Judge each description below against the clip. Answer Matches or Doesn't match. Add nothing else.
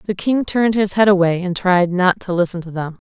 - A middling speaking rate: Doesn't match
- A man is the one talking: Doesn't match